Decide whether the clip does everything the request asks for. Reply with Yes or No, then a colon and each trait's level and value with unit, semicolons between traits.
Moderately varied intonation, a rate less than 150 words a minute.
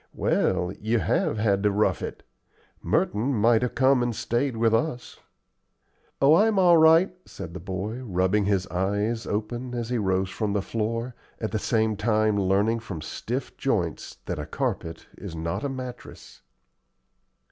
No: average, 3.8 semitones; average, 160 wpm